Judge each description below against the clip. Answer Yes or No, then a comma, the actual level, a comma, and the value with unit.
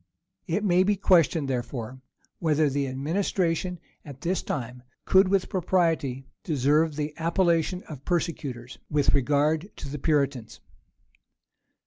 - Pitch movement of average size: Yes, average, 4.4 semitones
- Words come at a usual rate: No, slow, 120 wpm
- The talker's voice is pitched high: No, medium, 155 Hz